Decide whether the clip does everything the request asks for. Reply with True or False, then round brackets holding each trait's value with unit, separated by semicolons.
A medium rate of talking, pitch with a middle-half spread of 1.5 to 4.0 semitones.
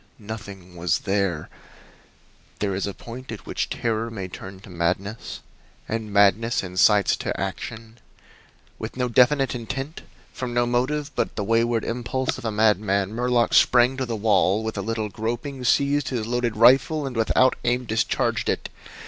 True (160 wpm; 3.3 semitones)